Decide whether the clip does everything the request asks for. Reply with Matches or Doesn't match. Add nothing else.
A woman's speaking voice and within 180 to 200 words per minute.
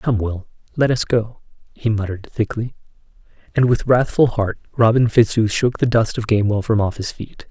Doesn't match